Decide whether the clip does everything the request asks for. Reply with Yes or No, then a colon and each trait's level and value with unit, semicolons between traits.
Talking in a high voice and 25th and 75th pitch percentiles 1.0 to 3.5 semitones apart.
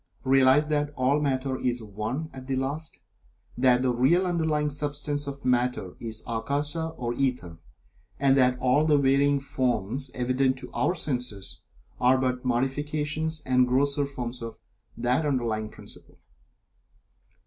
No: low, 130 Hz; average, 2.7 semitones